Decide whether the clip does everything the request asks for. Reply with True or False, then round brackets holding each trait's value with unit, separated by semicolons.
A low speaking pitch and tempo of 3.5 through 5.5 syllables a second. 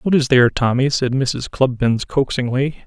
True (130 Hz; 5.2 syllables/s)